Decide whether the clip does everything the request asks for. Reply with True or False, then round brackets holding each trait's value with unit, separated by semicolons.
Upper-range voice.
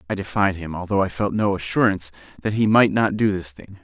False (95 Hz)